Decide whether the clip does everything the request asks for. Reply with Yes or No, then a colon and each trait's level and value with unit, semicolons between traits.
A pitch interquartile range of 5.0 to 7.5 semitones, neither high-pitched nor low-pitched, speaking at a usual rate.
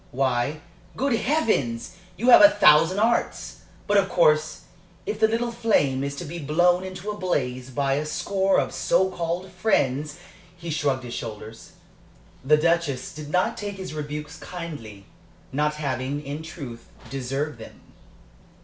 Yes: wide, 5.4 semitones; medium, 155 Hz; average, 155 wpm